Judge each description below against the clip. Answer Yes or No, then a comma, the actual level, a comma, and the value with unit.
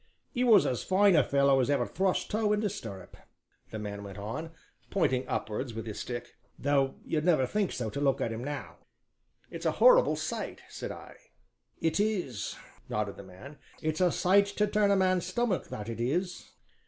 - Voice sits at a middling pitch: Yes, medium, 145 Hz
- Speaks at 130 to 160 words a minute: No, average, 190 wpm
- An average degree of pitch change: No, wide, 8.6 semitones